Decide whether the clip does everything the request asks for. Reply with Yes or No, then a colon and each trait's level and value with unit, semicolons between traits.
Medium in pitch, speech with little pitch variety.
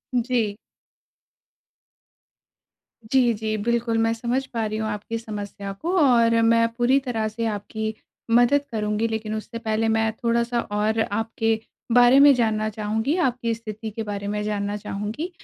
No: high, 225 Hz; narrow, 1.7 semitones